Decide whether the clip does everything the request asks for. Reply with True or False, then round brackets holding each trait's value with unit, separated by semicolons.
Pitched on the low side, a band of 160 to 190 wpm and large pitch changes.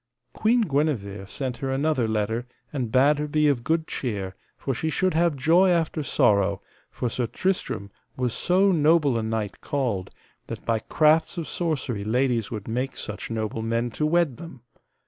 True (130 Hz; 170 wpm; 5.9 semitones)